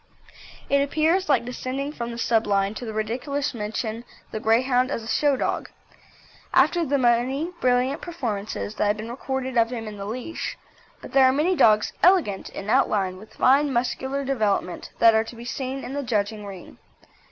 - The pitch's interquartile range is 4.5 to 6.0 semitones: No, average, 3.9 semitones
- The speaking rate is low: No, average, 185 wpm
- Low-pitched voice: No, high, 245 Hz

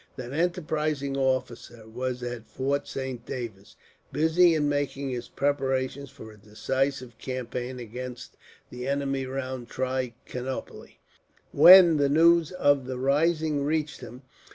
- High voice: No, low, 135 Hz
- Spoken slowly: Yes, slow, 125 wpm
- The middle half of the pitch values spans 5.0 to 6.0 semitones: No, narrow, 2.6 semitones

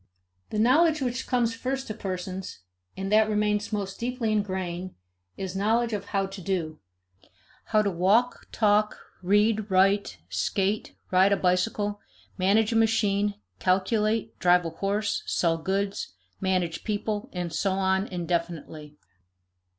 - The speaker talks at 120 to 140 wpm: Yes, slow, 135 wpm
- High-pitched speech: Yes, high, 200 Hz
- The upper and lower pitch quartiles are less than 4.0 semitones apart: Yes, narrow, 2.5 semitones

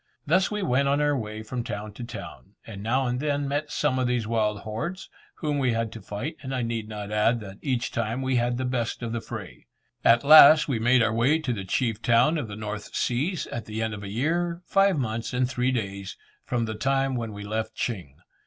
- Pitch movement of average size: Yes, average, 3.9 semitones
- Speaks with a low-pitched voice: Yes, low, 120 Hz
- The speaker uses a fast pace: Yes, fast, 235 wpm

